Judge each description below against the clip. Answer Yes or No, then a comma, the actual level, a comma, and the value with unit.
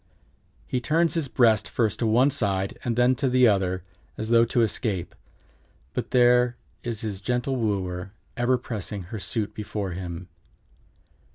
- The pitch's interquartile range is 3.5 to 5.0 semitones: Yes, average, 4.0 semitones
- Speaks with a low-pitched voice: Yes, low, 115 Hz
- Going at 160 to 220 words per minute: No, average, 150 wpm